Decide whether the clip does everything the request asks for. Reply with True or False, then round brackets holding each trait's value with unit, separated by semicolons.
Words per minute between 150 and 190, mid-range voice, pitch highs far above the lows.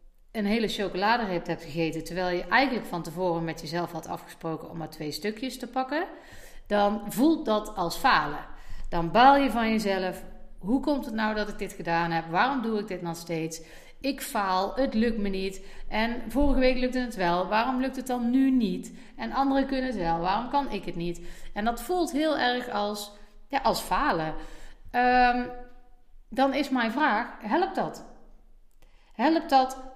False (180 wpm; 215 Hz; 6.2 semitones)